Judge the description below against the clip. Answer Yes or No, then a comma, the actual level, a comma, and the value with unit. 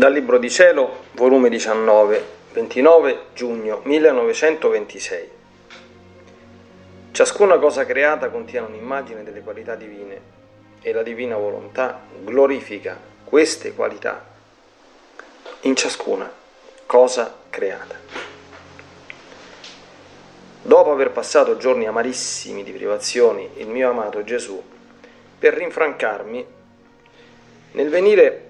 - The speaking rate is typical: No, slow, 90 wpm